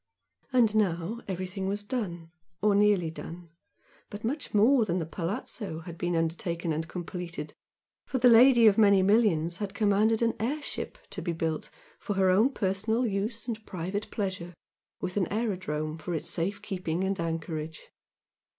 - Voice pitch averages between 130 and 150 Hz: No, high, 195 Hz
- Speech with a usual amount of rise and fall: Yes, average, 4.2 semitones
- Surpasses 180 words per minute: No, average, 160 wpm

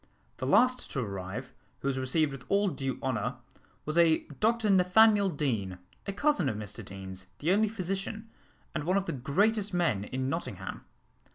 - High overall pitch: No, medium, 155 Hz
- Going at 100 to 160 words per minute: No, average, 170 wpm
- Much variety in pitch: Yes, wide, 8.1 semitones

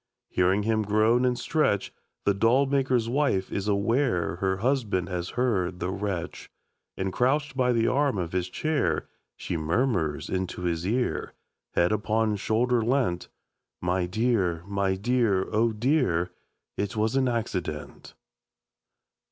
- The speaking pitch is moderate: No, low, 105 Hz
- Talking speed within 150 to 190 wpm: No, slow, 135 wpm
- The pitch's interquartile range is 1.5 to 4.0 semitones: No, average, 5.1 semitones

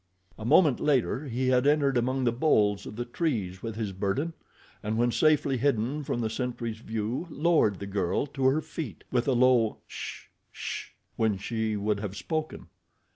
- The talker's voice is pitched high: No, low, 120 Hz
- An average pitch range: Yes, average, 4.4 semitones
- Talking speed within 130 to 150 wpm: No, average, 180 wpm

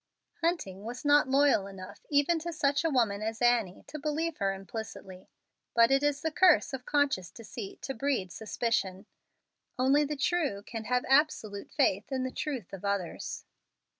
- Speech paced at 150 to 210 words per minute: Yes, average, 165 wpm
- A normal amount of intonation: No, wide, 6.3 semitones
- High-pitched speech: Yes, very high, 250 Hz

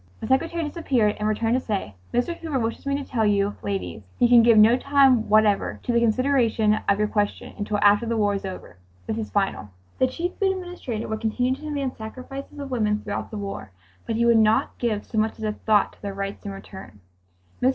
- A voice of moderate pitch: No, high, 225 Hz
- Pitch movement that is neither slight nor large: Yes, average, 3.8 semitones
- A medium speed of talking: No, fast, 225 wpm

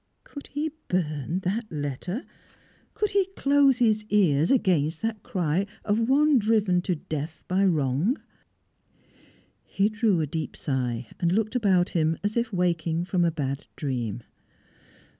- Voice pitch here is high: No, medium, 180 Hz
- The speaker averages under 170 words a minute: Yes, average, 140 wpm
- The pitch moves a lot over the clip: Yes, wide, 6.2 semitones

